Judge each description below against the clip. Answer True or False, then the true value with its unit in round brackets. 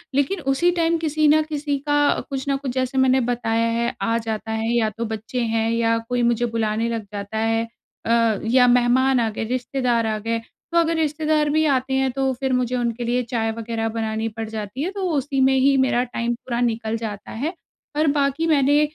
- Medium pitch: False (245 Hz)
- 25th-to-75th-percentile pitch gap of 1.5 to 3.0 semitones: False (3.4 semitones)